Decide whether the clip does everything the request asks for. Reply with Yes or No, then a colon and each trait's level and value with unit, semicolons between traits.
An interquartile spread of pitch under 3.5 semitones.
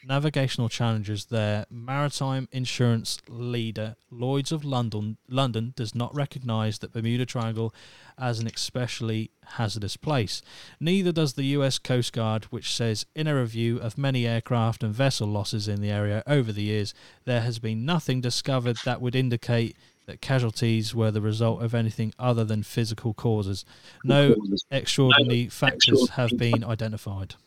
Yes: average, 2.8 semitones